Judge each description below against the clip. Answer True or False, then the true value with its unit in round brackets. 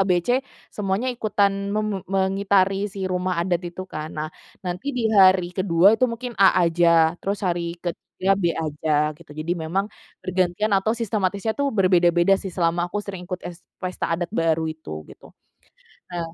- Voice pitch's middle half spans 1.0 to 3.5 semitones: True (2.5 semitones)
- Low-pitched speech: False (185 Hz)